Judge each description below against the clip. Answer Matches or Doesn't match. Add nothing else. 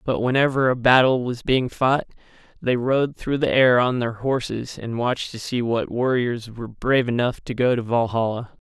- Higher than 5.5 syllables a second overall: Doesn't match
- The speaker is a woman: Doesn't match